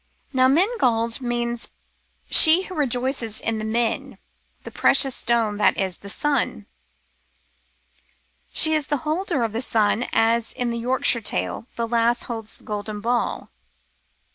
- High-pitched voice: Yes, high, 235 Hz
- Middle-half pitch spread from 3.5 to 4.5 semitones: No, average, 2.9 semitones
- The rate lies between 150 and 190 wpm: No, average, 140 wpm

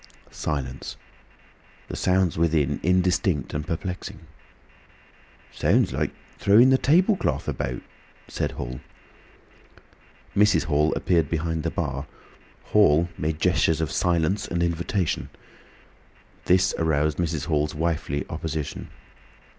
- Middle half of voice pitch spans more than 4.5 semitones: No, average, 3.3 semitones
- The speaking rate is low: Yes, slow, 105 wpm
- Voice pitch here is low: Yes, very low, 80 Hz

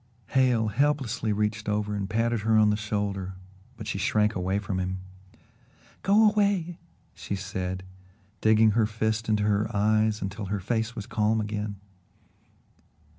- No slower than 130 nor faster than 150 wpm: Yes, average, 145 wpm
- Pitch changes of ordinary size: No, narrow, 1.6 semitones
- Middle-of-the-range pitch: No, low, 105 Hz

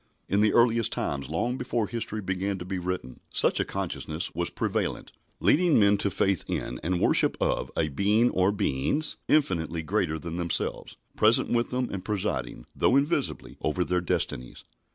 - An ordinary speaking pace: Yes, average, 170 wpm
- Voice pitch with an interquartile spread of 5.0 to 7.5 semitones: Yes, wide, 5.5 semitones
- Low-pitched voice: Yes, very low, 95 Hz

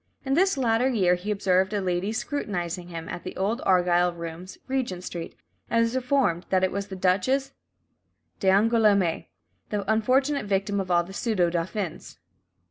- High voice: Yes, high, 195 Hz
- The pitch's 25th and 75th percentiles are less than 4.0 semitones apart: No, average, 4.3 semitones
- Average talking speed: Yes, average, 160 wpm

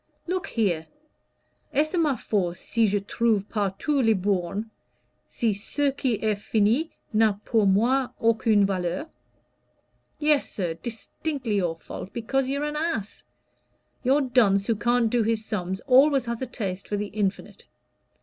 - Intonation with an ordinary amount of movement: Yes, average, 4.8 semitones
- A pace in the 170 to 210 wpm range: No, average, 150 wpm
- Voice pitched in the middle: No, high, 225 Hz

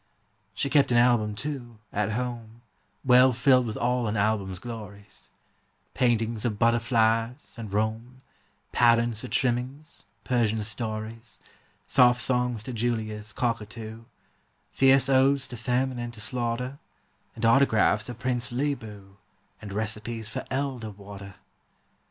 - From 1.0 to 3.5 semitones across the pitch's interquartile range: Yes, narrow, 2.4 semitones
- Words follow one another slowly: Yes, slow, 125 wpm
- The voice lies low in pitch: Yes, low, 115 Hz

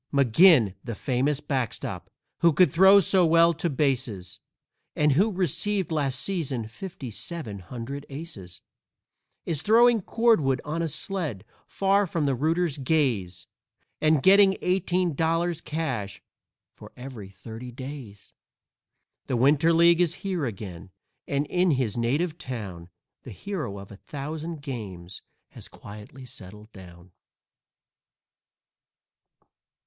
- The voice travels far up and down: Yes, wide, 7.0 semitones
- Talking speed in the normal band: No, slow, 125 wpm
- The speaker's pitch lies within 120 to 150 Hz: Yes, medium, 140 Hz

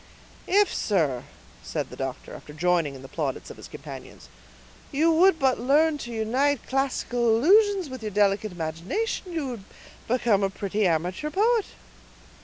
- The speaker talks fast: No, average, 155 wpm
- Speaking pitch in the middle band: No, high, 235 Hz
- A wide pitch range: Yes, wide, 8.9 semitones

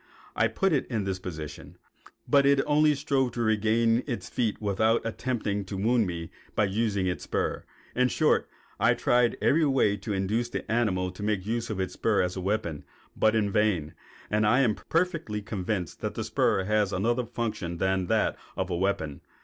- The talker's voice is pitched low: Yes, low, 105 Hz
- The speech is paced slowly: No, average, 190 wpm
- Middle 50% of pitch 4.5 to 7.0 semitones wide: No, average, 3.9 semitones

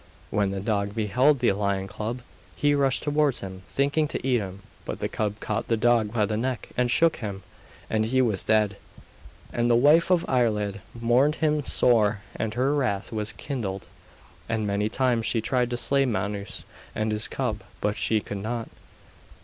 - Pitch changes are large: No, average, 3.8 semitones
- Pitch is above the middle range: No, low, 115 Hz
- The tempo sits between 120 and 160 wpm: No, average, 180 wpm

